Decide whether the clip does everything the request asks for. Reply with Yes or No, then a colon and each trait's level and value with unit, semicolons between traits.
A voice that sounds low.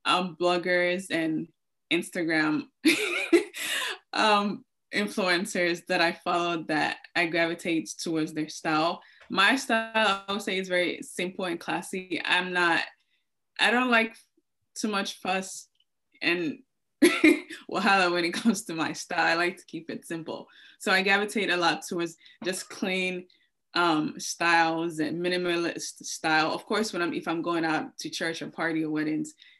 No: medium, 180 Hz